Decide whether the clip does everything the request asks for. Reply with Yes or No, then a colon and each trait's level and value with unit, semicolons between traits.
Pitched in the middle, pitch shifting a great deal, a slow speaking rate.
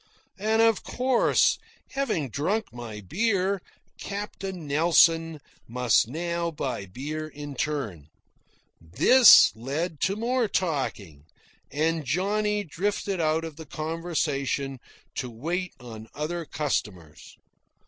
Yes: medium, 160 Hz; wide, 6.2 semitones; slow, 105 wpm